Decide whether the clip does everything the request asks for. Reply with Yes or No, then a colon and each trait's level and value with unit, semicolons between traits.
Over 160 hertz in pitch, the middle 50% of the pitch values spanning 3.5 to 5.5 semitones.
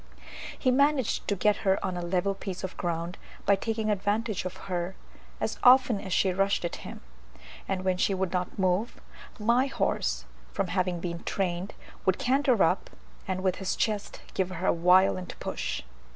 No: high, 190 Hz; narrow, 2.6 semitones